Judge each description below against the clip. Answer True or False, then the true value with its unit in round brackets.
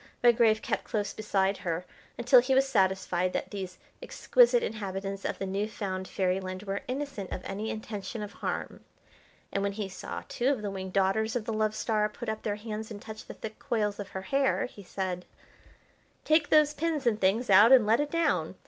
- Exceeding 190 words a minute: True (200 wpm)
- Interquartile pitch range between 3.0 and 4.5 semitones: True (3.6 semitones)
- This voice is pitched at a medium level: False (210 Hz)